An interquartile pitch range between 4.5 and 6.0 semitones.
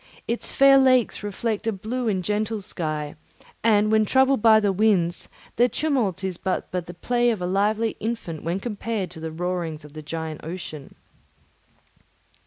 Yes: average, 4.8 semitones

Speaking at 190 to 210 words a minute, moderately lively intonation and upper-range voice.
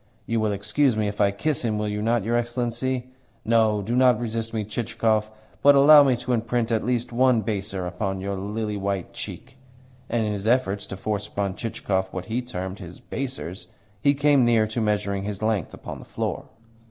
No: average, 200 wpm; average, 3.1 semitones; low, 110 Hz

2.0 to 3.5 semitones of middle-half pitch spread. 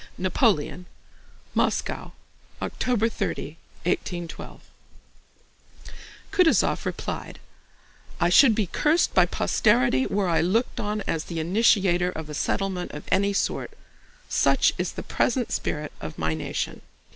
No: average, 5.0 semitones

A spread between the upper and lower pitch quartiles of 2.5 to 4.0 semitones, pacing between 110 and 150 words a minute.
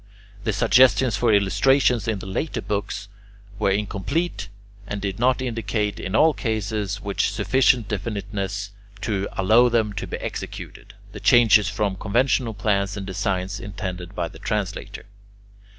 Yes: average, 2.8 semitones; average, 140 wpm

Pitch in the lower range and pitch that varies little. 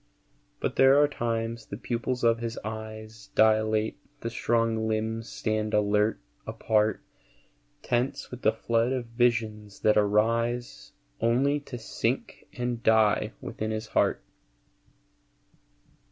Yes: low, 115 Hz; narrow, 1.5 semitones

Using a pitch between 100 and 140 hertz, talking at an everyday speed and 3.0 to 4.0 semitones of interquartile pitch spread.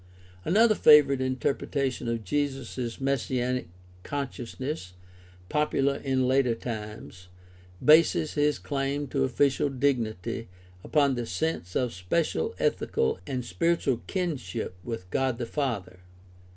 No: low, 135 Hz; slow, 110 wpm; average, 3.7 semitones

